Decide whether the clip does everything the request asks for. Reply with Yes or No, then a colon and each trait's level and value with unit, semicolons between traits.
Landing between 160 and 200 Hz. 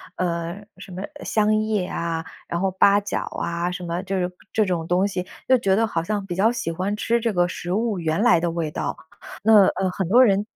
Yes: high, 190 Hz